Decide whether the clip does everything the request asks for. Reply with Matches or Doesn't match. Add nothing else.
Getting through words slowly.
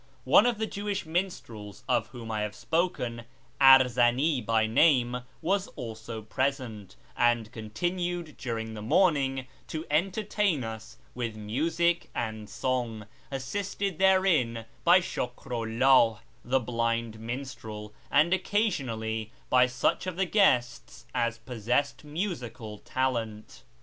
Matches